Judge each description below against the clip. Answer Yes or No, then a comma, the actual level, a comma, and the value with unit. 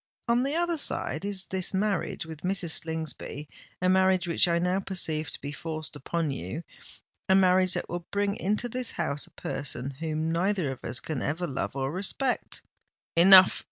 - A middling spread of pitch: Yes, average, 3.6 semitones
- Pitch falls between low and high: Yes, medium, 175 Hz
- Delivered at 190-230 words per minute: No, average, 170 wpm